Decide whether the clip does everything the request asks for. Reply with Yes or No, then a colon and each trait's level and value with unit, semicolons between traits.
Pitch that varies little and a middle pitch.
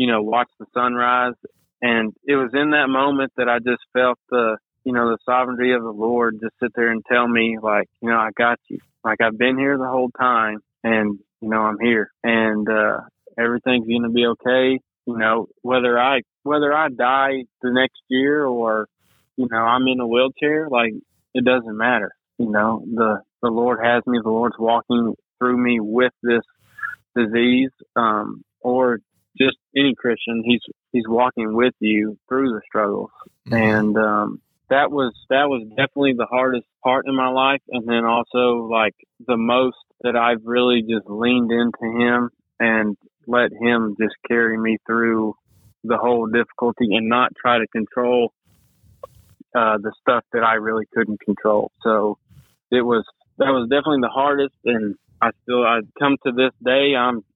No: narrow, 2.0 semitones; low, 120 Hz